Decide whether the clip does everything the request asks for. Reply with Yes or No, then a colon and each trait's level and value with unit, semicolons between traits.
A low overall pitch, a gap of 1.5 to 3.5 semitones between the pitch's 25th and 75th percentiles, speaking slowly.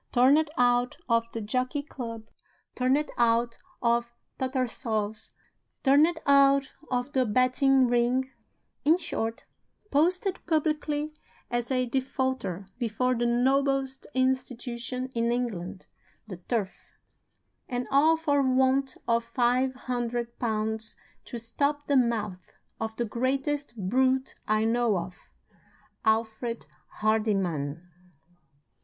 No: high, 245 Hz; average, 2.7 semitones; slow, 110 wpm